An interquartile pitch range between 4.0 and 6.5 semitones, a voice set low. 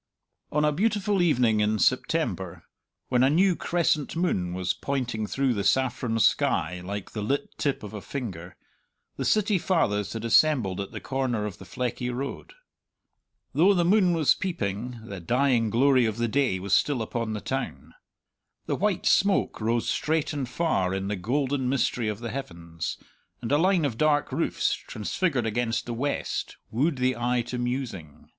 Yes: wide, 5.5 semitones; low, 125 Hz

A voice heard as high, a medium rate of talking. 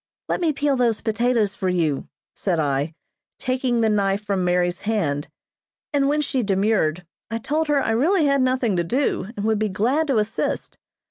Yes: high, 220 Hz; average, 185 wpm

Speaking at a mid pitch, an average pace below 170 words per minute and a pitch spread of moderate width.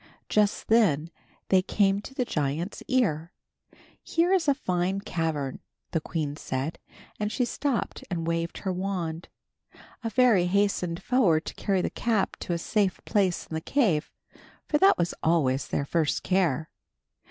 Yes: medium, 180 Hz; average, 155 wpm; average, 4.6 semitones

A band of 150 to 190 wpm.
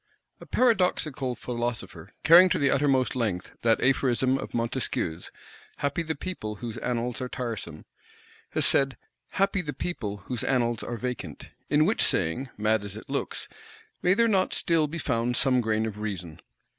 Yes: average, 160 wpm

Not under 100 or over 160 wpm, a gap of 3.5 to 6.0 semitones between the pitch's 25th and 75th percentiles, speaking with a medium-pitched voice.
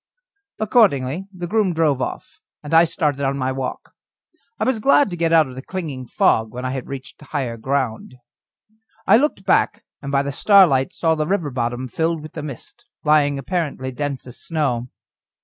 No: average, 180 wpm; average, 4.4 semitones; medium, 145 Hz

